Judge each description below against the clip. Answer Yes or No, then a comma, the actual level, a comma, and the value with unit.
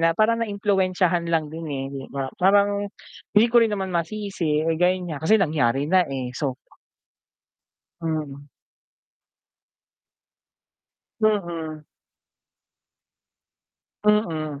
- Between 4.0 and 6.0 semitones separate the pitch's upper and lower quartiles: Yes, average, 5.0 semitones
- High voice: No, medium, 170 Hz